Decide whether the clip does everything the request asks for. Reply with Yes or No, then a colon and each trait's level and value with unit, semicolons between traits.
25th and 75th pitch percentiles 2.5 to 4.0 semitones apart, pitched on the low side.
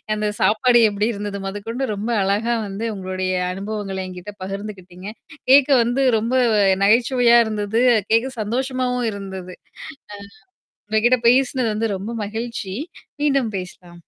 No: average, 3.6 semitones; high, 215 Hz